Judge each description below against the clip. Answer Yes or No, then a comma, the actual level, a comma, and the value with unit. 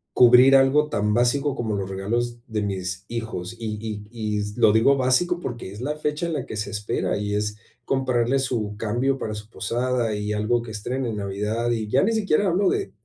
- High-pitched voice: No, low, 115 Hz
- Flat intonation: No, average, 4.1 semitones